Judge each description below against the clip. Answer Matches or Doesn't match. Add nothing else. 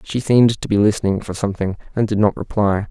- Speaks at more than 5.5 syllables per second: Matches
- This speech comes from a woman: Doesn't match